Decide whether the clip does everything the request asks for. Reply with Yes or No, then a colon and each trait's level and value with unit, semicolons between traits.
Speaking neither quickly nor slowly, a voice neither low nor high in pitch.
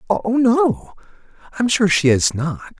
Yes: average, 150 wpm; medium, 170 Hz